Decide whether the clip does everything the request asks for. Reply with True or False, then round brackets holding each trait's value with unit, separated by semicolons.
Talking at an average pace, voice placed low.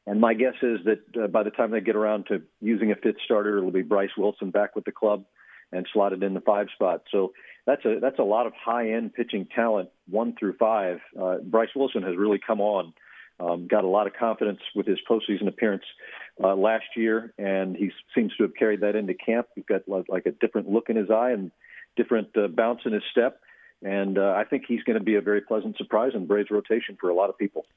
False (240 wpm; 105 Hz)